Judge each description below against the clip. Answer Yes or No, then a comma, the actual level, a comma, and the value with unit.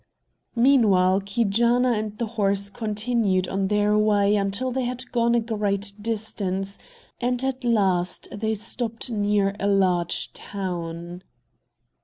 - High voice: Yes, high, 210 Hz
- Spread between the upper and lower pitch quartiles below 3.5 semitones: Yes, average, 3.0 semitones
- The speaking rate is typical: No, slow, 125 wpm